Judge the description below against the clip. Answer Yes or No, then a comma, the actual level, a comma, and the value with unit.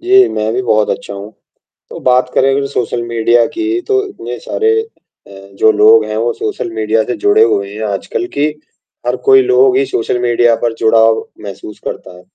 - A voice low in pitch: Yes, low, 120 Hz